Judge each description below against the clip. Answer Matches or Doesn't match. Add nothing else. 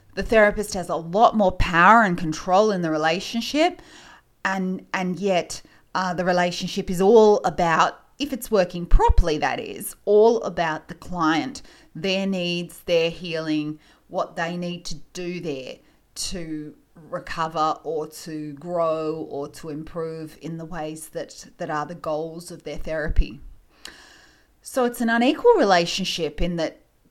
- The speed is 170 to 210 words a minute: Doesn't match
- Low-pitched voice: Doesn't match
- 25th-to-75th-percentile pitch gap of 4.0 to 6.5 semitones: Doesn't match